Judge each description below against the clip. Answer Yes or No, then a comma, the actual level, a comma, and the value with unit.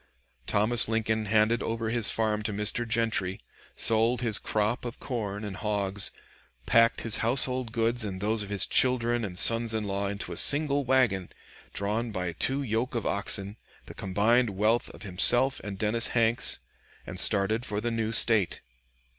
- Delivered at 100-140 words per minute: No, average, 165 wpm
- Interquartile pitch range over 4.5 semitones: No, narrow, 2.4 semitones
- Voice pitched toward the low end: Yes, low, 110 Hz